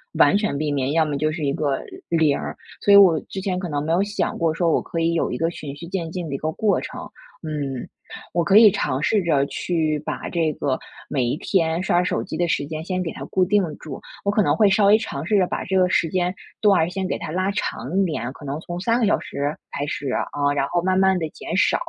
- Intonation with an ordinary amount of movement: Yes, average, 4.0 semitones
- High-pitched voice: No, medium, 170 Hz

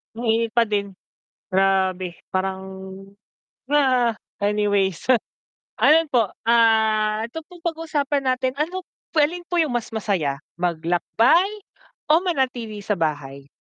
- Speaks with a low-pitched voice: No, high, 225 Hz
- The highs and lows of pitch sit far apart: Yes, wide, 7.0 semitones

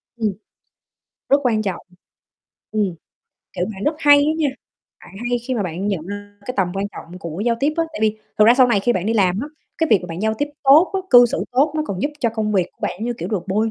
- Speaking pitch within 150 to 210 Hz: No, high, 220 Hz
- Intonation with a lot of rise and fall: No, average, 4.4 semitones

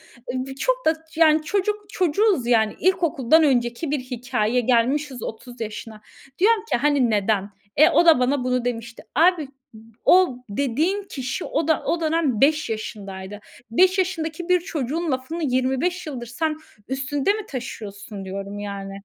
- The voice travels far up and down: Yes, wide, 5.9 semitones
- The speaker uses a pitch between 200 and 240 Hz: No, very high, 270 Hz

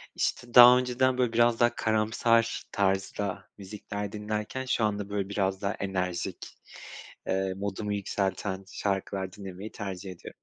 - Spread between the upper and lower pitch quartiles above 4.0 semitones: No, average, 2.8 semitones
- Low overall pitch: Yes, low, 100 Hz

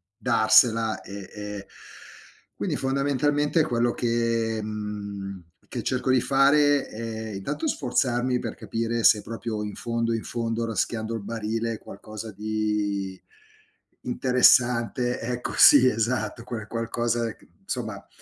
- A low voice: Yes, low, 115 Hz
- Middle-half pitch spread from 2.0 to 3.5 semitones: Yes, narrow, 2.4 semitones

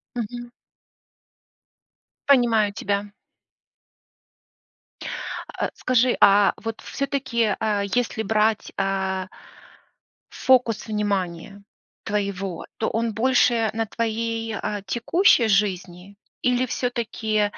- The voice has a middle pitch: No, high, 220 Hz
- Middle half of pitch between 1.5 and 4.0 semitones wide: Yes, average, 2.8 semitones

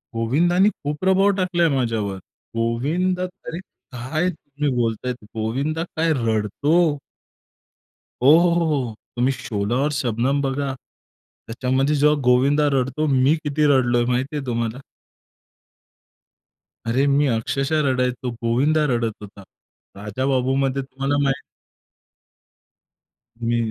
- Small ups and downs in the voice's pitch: No, average, 4.1 semitones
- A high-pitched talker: No, low, 135 Hz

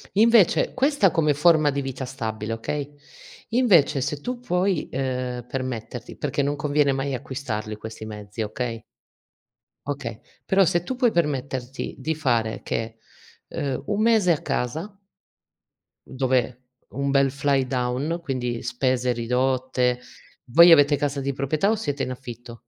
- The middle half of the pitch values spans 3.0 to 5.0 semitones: Yes, average, 4.1 semitones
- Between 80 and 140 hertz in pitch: Yes, low, 135 Hz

